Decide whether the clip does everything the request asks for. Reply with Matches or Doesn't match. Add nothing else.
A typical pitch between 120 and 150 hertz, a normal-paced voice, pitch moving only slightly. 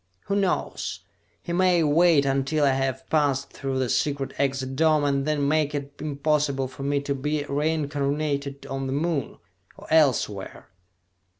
Matches